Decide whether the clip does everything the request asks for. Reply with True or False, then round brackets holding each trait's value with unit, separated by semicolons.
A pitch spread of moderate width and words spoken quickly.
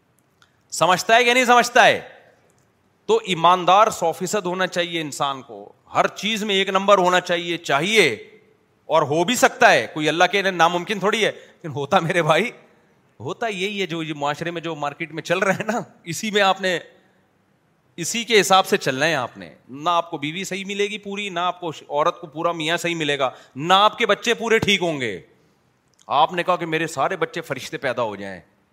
True (3.7 semitones; 210 wpm)